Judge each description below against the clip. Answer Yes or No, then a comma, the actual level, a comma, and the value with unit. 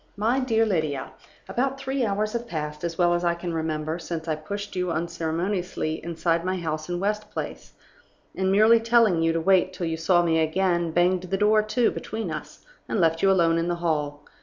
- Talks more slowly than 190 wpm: No, fast, 205 wpm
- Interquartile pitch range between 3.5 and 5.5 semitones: Yes, average, 4.0 semitones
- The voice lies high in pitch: No, medium, 175 Hz